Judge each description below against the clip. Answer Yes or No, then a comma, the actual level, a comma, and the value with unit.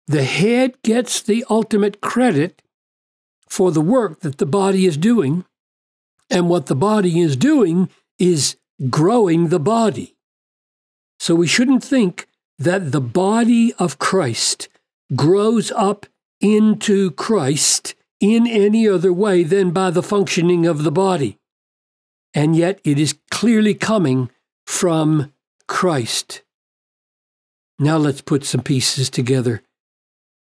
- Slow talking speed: Yes, slow, 120 wpm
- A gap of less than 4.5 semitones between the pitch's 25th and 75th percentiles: No, average, 5.3 semitones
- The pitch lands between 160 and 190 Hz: Yes, medium, 185 Hz